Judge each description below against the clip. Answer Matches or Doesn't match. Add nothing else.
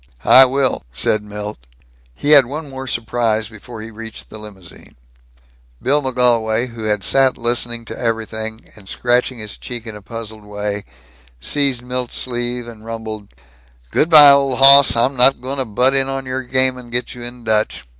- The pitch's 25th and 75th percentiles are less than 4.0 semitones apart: Matches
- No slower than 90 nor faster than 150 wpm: Doesn't match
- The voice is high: Doesn't match